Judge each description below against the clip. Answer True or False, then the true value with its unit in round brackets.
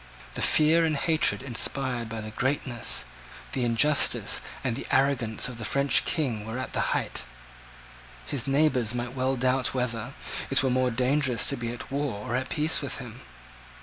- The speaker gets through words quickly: False (175 wpm)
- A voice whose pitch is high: False (130 Hz)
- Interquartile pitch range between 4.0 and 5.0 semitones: False (2.7 semitones)